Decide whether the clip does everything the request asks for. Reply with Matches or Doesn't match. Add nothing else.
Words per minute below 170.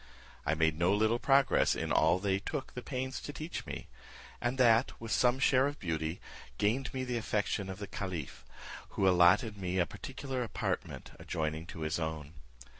Doesn't match